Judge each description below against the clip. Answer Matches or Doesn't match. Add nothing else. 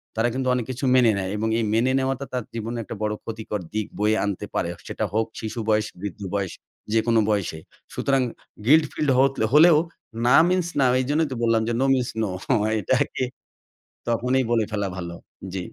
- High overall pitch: Doesn't match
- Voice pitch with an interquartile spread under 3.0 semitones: Doesn't match